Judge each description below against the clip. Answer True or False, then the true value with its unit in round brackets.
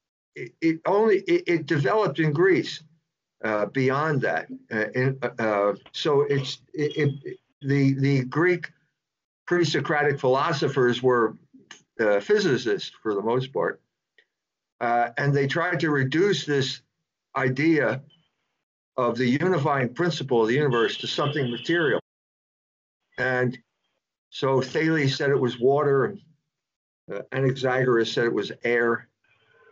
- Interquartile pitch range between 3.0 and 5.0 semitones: True (4.3 semitones)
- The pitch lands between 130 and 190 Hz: True (140 Hz)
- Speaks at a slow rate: True (120 wpm)